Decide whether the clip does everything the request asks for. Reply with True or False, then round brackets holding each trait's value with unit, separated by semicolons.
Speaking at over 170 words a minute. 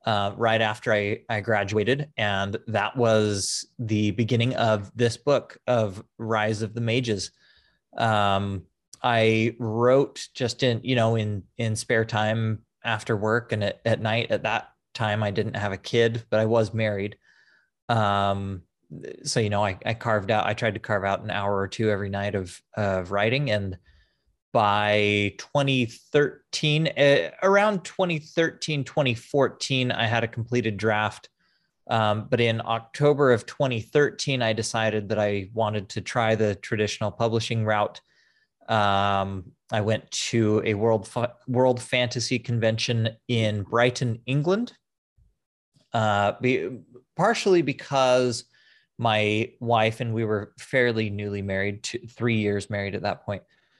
False (145 wpm)